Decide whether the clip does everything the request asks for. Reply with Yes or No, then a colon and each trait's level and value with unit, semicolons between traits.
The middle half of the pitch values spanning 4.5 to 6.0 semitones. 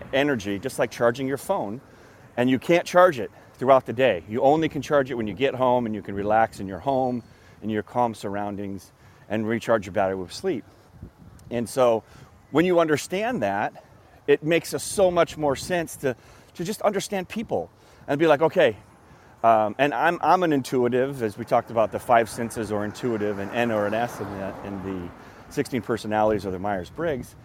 Yes: average, 4.9 semitones